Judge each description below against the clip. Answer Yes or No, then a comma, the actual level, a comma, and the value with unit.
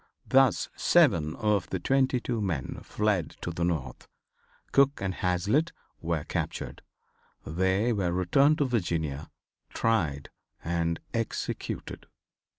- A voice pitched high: No, very low, 95 Hz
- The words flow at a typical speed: No, slow, 115 wpm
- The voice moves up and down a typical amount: No, wide, 5.7 semitones